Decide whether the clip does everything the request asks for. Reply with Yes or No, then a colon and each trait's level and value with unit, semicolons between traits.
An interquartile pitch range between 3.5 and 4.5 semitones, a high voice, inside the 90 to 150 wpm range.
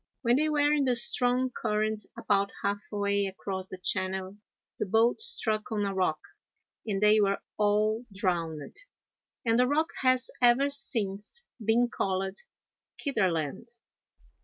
Yes: average, 4.1 semitones; high, 210 Hz; slow, 135 wpm